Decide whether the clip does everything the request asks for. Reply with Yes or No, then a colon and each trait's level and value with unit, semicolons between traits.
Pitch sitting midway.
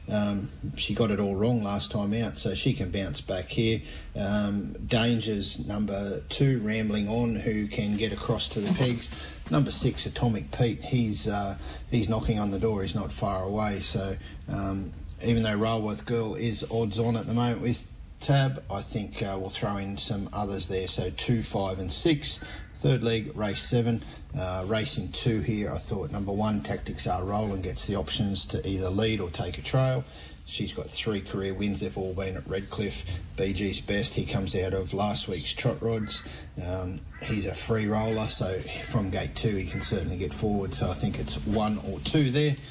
No: low, 105 Hz